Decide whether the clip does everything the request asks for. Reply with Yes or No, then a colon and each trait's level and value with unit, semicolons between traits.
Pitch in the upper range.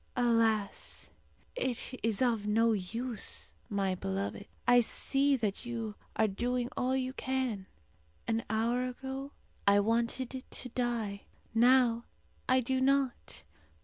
Yes: high, 235 Hz